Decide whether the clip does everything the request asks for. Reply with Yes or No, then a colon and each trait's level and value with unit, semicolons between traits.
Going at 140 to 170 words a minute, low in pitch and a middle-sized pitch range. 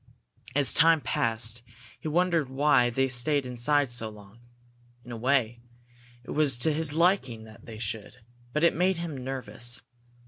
Yes: average, 160 wpm; low, 130 Hz; average, 4.4 semitones